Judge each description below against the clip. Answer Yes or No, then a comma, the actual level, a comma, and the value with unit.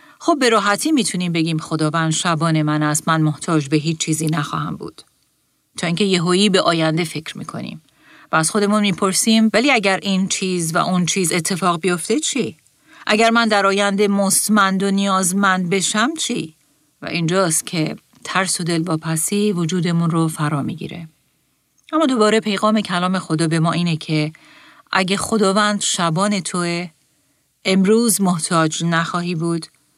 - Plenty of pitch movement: No, average, 3.8 semitones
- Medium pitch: Yes, medium, 180 Hz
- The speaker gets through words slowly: No, average, 150 wpm